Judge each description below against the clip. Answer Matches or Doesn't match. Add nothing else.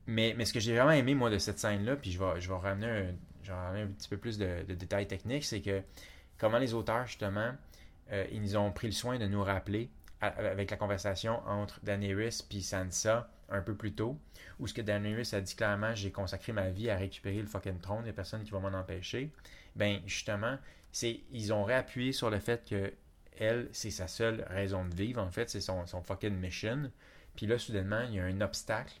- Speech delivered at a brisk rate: Matches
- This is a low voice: Matches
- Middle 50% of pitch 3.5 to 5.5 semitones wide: Doesn't match